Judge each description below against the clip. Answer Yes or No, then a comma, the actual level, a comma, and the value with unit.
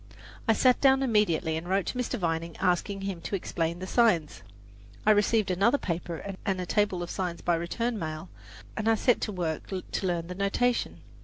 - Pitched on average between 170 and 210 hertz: Yes, high, 190 Hz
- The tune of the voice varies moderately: Yes, average, 4.1 semitones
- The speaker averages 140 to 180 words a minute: No, average, 190 wpm